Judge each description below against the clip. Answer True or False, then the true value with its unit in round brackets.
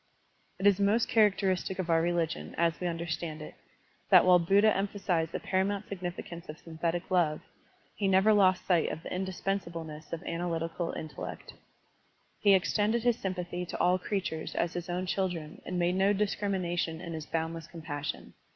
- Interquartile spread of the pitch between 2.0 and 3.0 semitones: True (2.6 semitones)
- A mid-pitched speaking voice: True (175 Hz)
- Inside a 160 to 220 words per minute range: True (170 wpm)